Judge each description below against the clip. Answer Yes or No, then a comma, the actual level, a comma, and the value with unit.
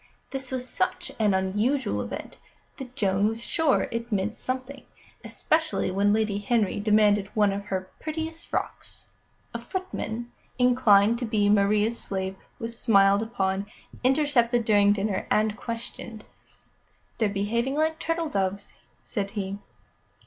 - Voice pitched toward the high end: Yes, high, 220 Hz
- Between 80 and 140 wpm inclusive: Yes, slow, 135 wpm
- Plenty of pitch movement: No, average, 3.8 semitones